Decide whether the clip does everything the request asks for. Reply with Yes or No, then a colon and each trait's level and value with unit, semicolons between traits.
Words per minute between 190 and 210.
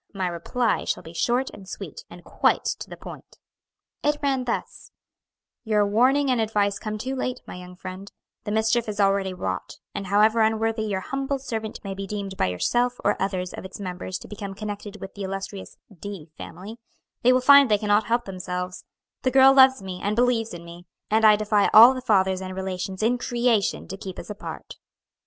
Yes: average, 195 wpm